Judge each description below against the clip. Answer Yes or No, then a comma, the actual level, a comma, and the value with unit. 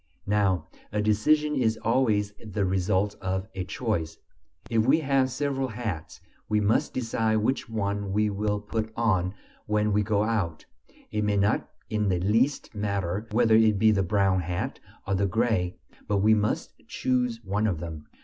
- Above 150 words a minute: Yes, average, 170 wpm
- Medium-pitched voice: No, low, 105 Hz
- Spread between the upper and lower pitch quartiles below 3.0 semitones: Yes, narrow, 2.5 semitones